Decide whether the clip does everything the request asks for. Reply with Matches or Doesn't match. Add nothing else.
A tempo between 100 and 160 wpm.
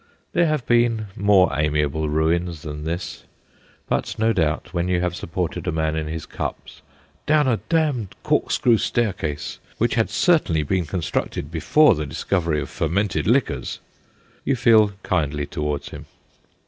Matches